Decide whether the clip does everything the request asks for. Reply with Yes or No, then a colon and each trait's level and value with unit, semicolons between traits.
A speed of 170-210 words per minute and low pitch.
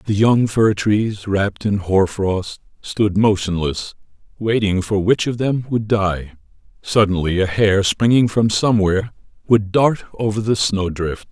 No: average, 150 wpm; low, 105 Hz